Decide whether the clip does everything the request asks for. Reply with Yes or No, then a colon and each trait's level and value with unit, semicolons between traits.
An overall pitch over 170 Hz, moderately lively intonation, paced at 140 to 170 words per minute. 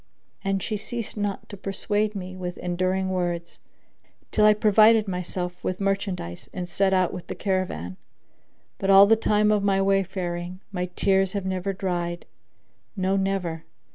No: high, 190 Hz; narrow, 1.9 semitones; average, 155 wpm